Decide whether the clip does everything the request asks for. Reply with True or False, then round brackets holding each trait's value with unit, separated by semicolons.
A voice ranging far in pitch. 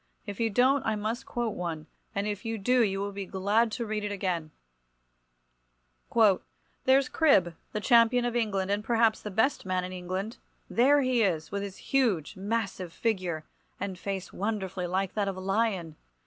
False (3.6 semitones)